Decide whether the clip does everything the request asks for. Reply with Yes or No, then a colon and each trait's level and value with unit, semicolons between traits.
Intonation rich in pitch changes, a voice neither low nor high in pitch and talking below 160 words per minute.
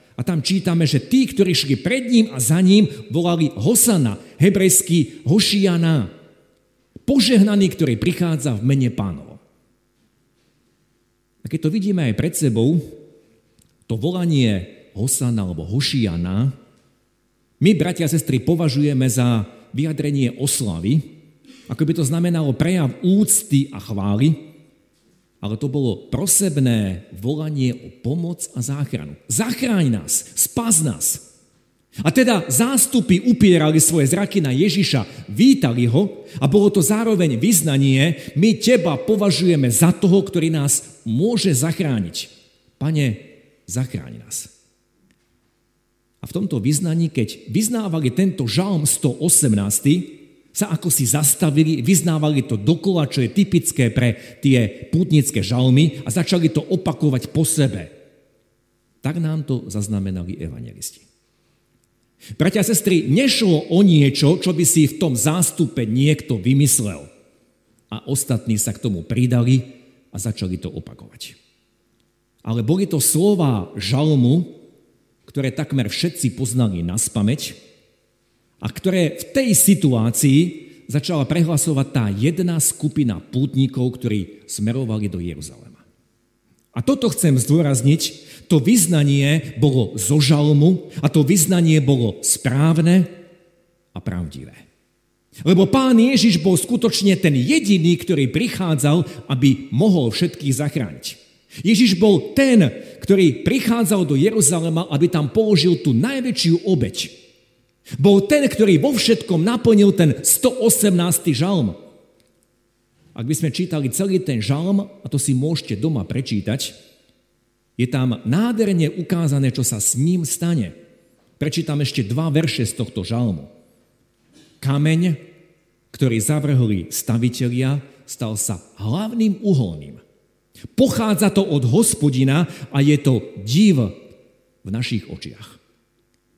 Yes: wide, 6.3 semitones; medium, 150 Hz; average, 120 wpm